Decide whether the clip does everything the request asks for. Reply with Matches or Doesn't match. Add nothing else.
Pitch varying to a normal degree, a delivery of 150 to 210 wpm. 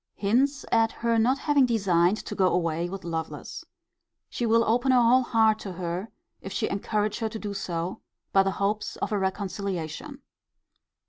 Matches